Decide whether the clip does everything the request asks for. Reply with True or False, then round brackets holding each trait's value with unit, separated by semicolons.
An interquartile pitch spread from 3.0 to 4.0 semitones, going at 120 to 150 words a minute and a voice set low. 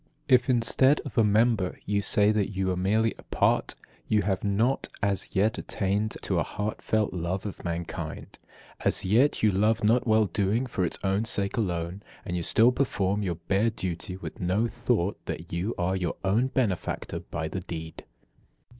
False (3.4 semitones; 180 wpm; 100 Hz)